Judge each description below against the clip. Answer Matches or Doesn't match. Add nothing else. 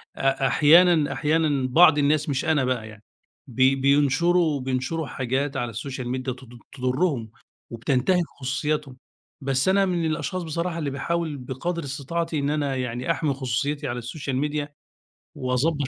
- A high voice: Doesn't match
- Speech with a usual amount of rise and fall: Matches